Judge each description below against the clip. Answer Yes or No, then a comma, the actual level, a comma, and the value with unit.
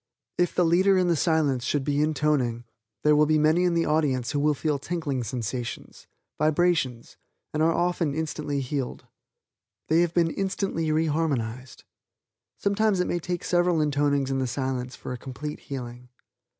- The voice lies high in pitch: No, medium, 150 Hz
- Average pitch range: Yes, average, 4.1 semitones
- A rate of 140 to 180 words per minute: Yes, average, 165 wpm